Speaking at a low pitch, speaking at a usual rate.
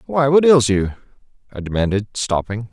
Yes: low, 115 Hz; average, 155 wpm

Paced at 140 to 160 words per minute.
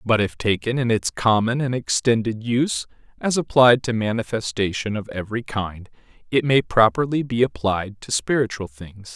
Yes: average, 155 wpm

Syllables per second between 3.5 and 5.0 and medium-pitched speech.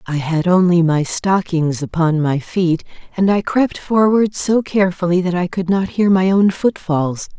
Yes: 4.4 syllables/s; medium, 180 Hz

